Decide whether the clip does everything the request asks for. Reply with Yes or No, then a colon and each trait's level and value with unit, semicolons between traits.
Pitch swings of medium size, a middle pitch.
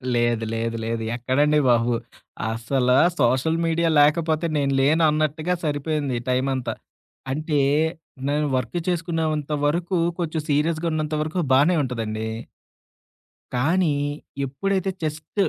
Yes: average, 4.1 semitones; medium, 150 Hz